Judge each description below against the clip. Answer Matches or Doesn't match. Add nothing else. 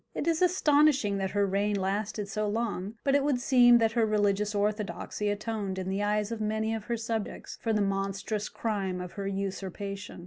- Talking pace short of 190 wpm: Doesn't match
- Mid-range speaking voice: Doesn't match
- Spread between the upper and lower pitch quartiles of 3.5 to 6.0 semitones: Doesn't match